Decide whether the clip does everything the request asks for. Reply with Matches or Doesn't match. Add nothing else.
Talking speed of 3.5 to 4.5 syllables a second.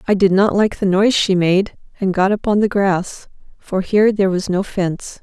Doesn't match